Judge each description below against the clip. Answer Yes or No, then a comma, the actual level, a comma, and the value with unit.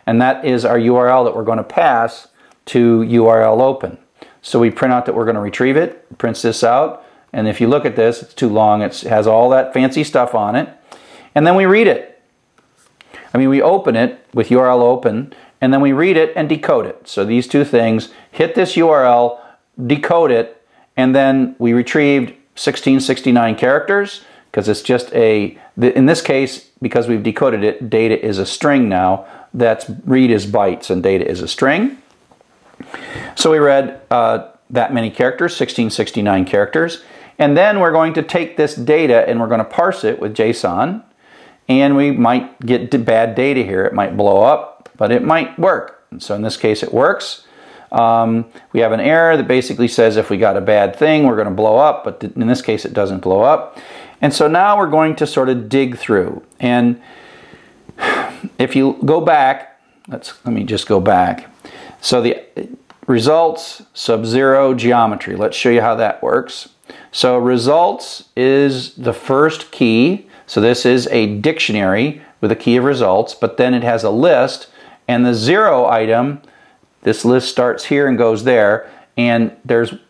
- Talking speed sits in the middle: Yes, average, 185 wpm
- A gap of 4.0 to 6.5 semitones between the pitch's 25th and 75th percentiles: No, average, 3.2 semitones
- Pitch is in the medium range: No, low, 120 Hz